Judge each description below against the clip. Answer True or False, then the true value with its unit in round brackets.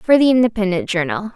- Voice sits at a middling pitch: False (205 Hz)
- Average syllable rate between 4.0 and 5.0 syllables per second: False (6.1 syllables/s)